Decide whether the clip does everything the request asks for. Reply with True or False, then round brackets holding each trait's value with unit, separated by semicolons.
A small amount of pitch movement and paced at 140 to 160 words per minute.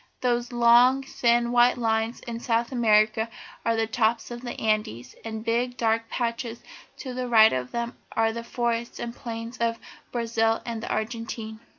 False (1.2 semitones; 175 wpm)